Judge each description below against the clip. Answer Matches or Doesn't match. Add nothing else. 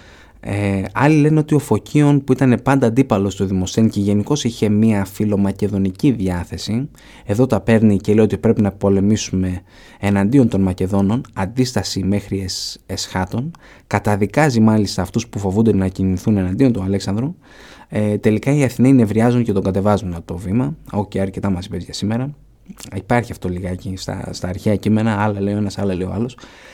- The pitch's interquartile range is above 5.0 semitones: Doesn't match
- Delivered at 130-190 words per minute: Matches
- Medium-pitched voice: Doesn't match